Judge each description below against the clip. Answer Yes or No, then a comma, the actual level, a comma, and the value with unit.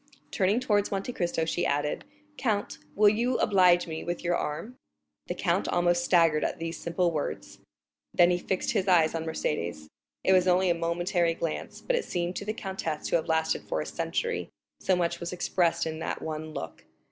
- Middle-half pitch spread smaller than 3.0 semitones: Yes, narrow, 2.6 semitones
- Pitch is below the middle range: No, medium, 175 Hz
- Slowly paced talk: No, average, 195 wpm